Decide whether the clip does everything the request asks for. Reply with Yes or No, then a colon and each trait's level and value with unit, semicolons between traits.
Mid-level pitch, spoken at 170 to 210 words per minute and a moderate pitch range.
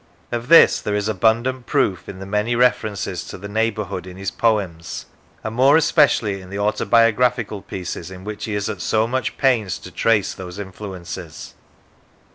No: low, 105 Hz; average, 175 wpm; average, 3.5 semitones